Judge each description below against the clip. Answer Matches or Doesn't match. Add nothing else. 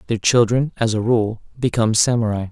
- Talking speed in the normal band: Matches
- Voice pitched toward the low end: Matches